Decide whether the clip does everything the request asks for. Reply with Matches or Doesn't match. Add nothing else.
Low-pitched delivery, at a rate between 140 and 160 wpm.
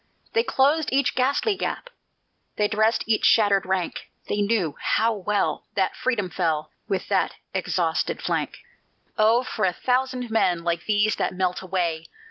Doesn't match